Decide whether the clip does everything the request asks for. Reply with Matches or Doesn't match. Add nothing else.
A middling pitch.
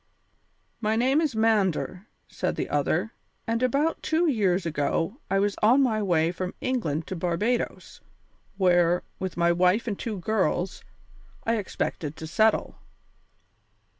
Doesn't match